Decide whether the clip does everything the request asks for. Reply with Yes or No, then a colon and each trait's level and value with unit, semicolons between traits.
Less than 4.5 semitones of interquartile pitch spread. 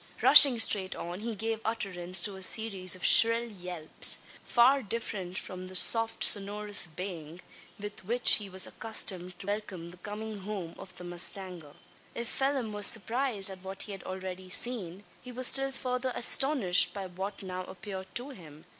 Yes: average, 3.7 semitones